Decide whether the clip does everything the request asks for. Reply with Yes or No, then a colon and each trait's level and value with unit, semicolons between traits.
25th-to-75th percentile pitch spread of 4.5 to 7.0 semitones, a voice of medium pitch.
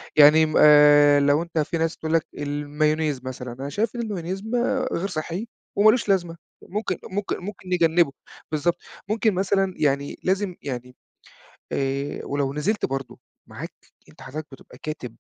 Yes: average, 4.8 semitones; medium, 160 Hz